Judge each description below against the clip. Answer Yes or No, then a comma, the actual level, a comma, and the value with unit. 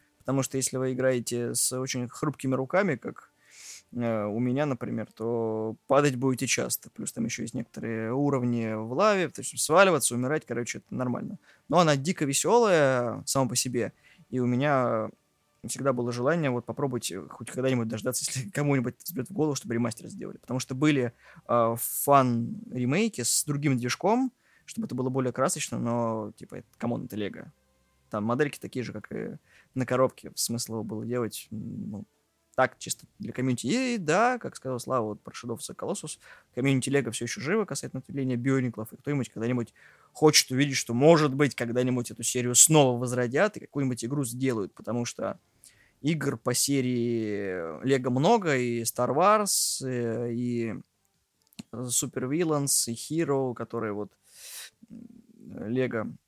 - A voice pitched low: Yes, low, 130 Hz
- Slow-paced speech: No, average, 155 wpm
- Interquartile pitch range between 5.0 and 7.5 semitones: No, average, 3.2 semitones